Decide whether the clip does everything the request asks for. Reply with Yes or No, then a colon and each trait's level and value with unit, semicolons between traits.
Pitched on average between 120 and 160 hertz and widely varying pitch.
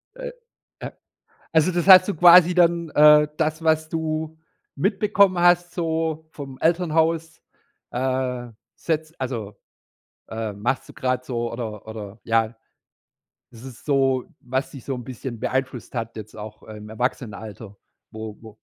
Yes: low, 135 Hz; wide, 6.1 semitones